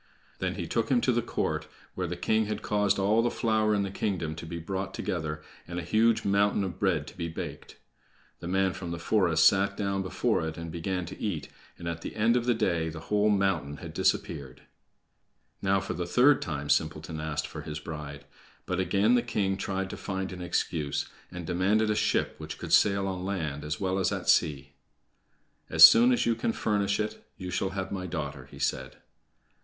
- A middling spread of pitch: Yes, average, 3.9 semitones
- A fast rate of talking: Yes, fast, 210 wpm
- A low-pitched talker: Yes, very low, 95 Hz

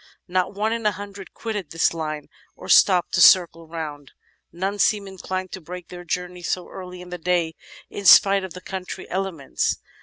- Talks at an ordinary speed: Yes, average, 185 wpm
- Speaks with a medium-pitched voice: Yes, medium, 180 Hz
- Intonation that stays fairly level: Yes, narrow, 2.3 semitones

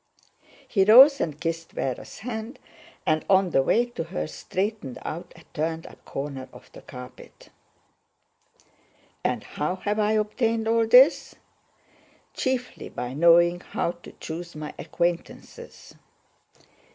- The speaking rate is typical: No, slow, 125 wpm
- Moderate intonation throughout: No, wide, 6.1 semitones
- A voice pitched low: No, medium, 175 Hz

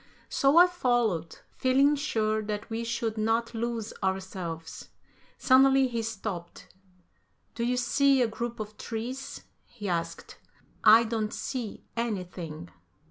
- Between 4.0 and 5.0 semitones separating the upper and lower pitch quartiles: No, average, 3.2 semitones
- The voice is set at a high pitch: Yes, high, 225 Hz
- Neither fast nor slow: No, slow, 125 wpm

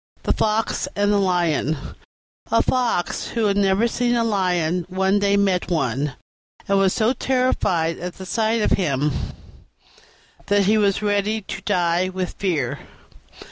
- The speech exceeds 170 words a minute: No, average, 150 wpm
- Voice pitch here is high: Yes, high, 195 Hz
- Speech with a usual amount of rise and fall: Yes, average, 3.3 semitones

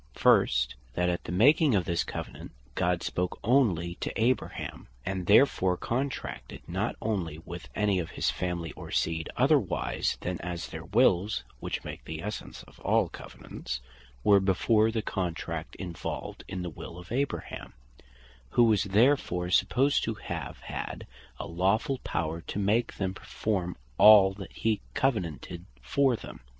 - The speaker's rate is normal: Yes, average, 150 wpm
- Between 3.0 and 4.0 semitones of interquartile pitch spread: No, average, 4.4 semitones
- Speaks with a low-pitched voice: Yes, very low, 95 Hz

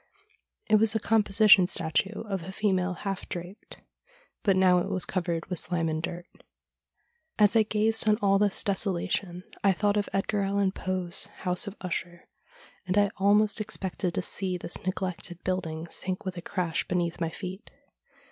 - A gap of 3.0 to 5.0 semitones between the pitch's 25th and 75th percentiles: No, narrow, 2.4 semitones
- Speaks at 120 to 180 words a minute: Yes, average, 170 wpm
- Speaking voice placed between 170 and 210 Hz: Yes, high, 190 Hz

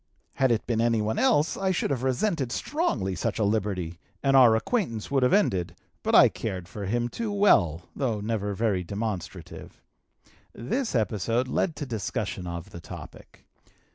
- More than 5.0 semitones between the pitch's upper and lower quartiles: Yes, wide, 5.6 semitones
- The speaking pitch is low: Yes, low, 115 Hz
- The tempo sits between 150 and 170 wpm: Yes, average, 165 wpm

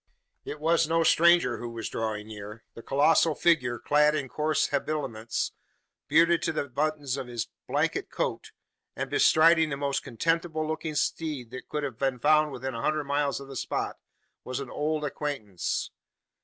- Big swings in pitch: No, average, 3.9 semitones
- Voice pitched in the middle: Yes, medium, 145 Hz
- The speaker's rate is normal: Yes, average, 170 wpm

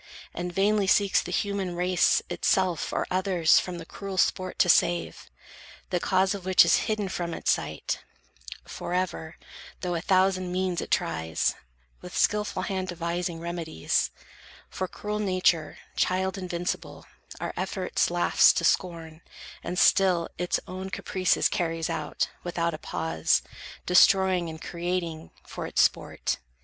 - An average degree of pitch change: No, narrow, 1.8 semitones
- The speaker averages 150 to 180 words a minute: No, average, 140 wpm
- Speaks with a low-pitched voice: No, medium, 180 Hz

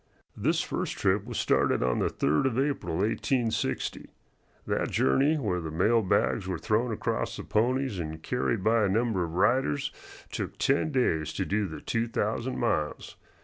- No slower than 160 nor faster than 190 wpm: Yes, average, 170 wpm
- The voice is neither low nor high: No, low, 105 Hz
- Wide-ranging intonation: Yes, wide, 6.0 semitones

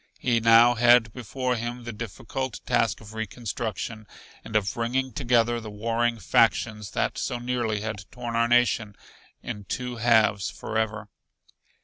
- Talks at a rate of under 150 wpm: Yes, average, 140 wpm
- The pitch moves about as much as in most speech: No, narrow, 2.0 semitones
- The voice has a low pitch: Yes, low, 115 Hz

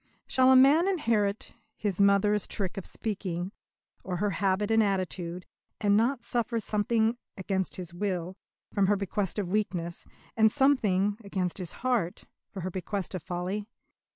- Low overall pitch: No, high, 200 Hz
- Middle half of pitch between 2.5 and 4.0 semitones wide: Yes, average, 3.0 semitones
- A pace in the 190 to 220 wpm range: No, average, 155 wpm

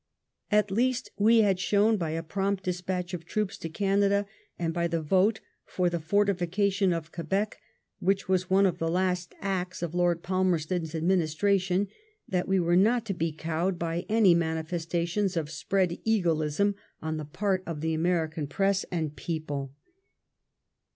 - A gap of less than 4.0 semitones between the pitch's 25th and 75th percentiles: Yes, average, 3.1 semitones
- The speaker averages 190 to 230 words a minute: No, average, 155 wpm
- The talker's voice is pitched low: No, medium, 180 Hz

